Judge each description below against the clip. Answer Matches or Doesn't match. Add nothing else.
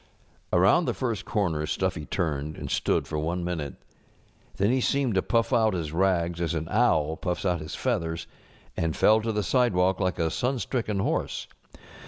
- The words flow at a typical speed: Matches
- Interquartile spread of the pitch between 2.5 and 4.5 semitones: Doesn't match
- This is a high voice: Doesn't match